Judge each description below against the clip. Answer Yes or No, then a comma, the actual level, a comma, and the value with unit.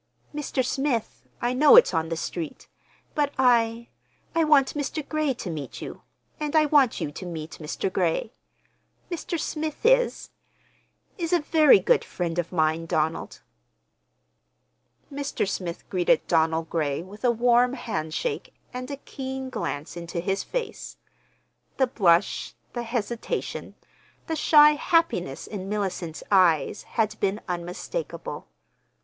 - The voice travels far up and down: Yes, wide, 9.0 semitones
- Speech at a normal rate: No, slow, 130 wpm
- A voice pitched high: Yes, high, 230 Hz